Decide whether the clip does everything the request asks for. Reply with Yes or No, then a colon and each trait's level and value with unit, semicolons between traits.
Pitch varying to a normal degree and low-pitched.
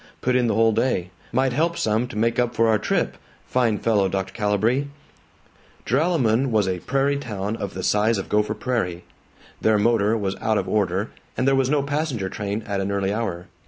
Yes: average, 3.9 semitones; low, 110 Hz